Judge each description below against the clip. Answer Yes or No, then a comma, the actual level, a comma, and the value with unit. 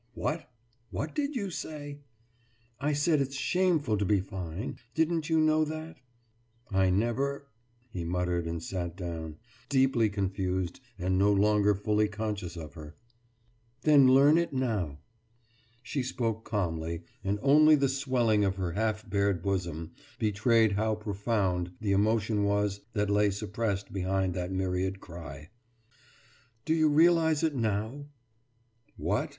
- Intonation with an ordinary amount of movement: No, wide, 6.5 semitones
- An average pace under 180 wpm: Yes, average, 140 wpm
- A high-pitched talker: No, low, 105 Hz